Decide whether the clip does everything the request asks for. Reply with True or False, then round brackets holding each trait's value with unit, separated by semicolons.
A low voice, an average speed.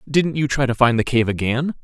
False (130 Hz; 260 wpm)